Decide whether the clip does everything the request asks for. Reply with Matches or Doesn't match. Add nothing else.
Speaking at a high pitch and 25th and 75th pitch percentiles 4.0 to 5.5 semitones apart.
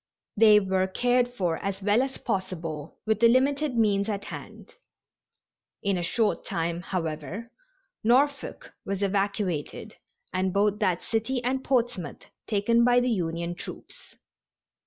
Matches